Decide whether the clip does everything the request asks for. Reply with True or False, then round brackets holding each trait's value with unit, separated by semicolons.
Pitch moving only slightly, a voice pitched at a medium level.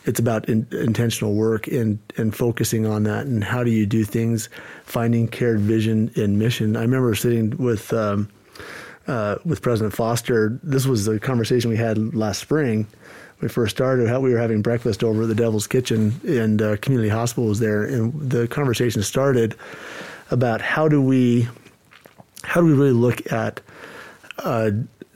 False (2.0 semitones; 115 Hz)